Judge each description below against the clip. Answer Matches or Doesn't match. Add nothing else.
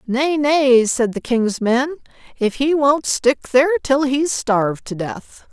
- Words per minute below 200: Matches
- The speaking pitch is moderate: Doesn't match